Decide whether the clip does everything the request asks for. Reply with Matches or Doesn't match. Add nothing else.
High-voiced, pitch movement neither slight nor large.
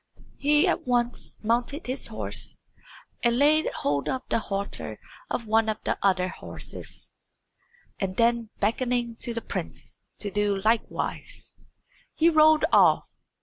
Matches